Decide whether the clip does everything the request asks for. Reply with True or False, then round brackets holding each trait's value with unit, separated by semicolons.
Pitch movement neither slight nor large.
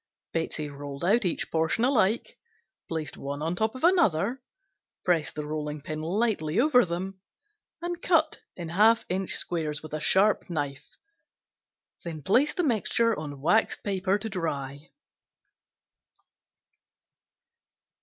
False (6.4 semitones)